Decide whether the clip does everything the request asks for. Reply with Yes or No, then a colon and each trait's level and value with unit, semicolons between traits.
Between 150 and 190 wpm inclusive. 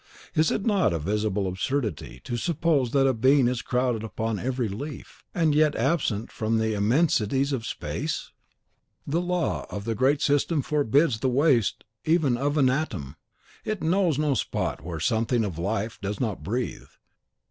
Yes: average, 160 wpm